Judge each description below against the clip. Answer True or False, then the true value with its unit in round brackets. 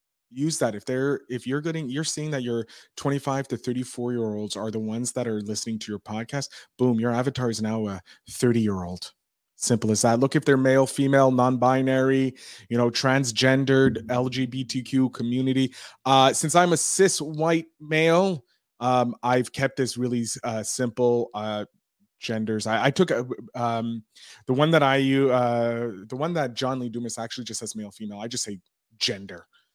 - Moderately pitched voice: False (125 Hz)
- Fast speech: False (185 wpm)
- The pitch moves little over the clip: False (3.1 semitones)